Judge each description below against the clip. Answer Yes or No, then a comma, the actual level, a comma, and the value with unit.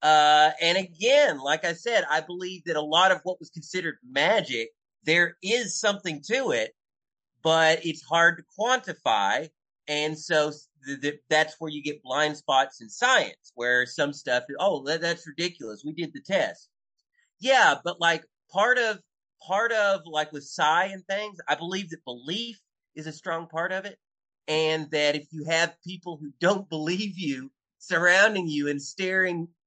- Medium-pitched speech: Yes, medium, 170 Hz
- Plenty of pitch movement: No, average, 4.0 semitones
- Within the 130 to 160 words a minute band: No, average, 170 wpm